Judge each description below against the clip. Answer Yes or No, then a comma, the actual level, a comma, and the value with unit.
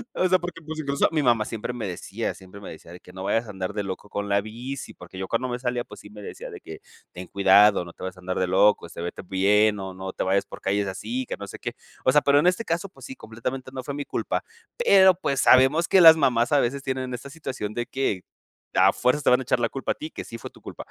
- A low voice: Yes, low, 120 Hz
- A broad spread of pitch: Yes, wide, 5.9 semitones